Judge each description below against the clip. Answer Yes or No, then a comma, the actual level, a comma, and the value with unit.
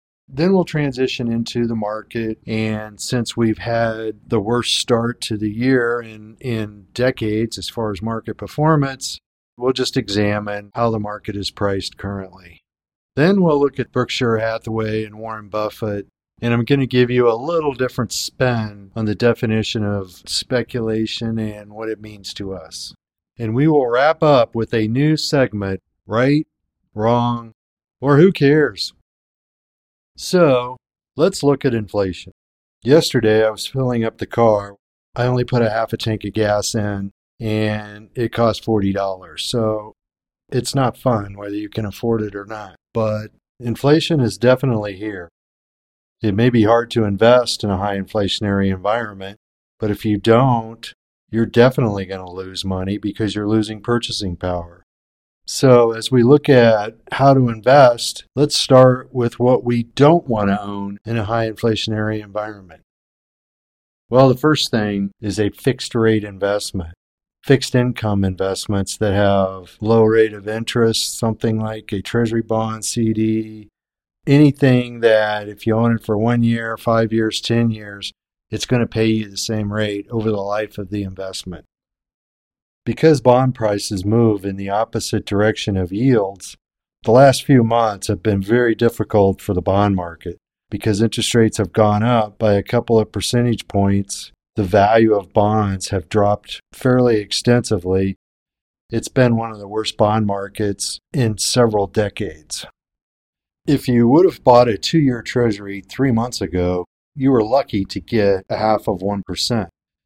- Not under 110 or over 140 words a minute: No, average, 160 wpm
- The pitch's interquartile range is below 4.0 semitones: Yes, average, 2.9 semitones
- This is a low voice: Yes, low, 110 Hz